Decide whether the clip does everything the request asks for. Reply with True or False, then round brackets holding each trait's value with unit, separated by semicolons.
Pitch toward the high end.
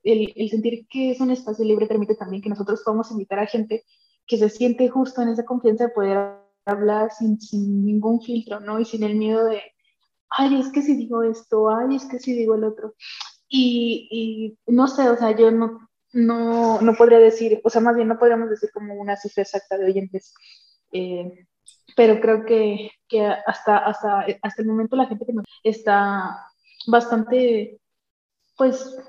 True (225 Hz)